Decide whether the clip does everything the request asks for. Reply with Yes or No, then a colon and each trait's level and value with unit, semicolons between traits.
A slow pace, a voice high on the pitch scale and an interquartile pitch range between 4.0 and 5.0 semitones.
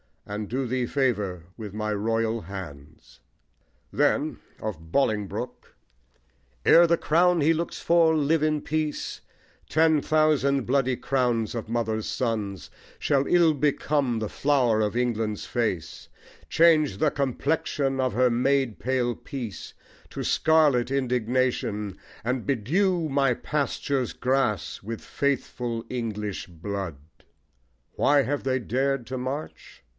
No: slow, 120 wpm; low, 125 Hz; average, 4.7 semitones